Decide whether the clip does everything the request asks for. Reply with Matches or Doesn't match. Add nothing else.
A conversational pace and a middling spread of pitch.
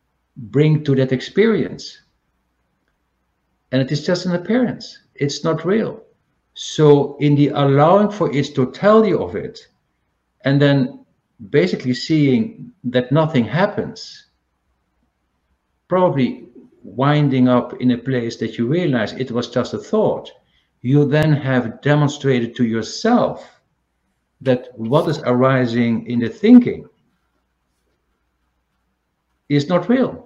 Doesn't match